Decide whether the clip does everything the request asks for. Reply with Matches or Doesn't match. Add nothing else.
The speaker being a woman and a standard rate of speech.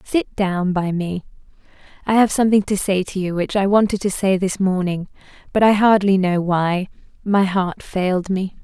Matches